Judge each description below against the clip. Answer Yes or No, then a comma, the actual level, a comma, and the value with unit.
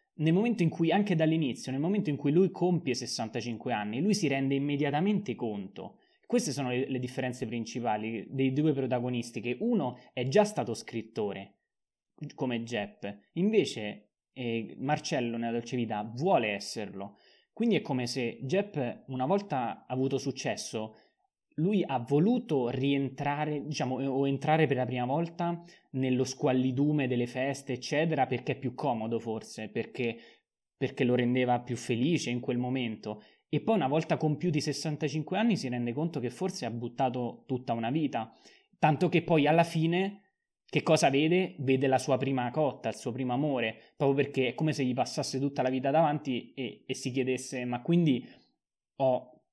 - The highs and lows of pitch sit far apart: No, average, 4.2 semitones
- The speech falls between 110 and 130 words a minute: No, average, 165 wpm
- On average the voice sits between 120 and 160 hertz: Yes, low, 135 Hz